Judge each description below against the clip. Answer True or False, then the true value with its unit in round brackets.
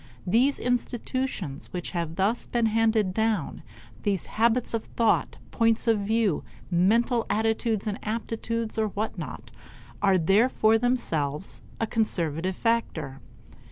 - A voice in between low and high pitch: False (220 Hz)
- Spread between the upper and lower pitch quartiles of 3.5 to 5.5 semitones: True (3.8 semitones)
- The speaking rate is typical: False (120 wpm)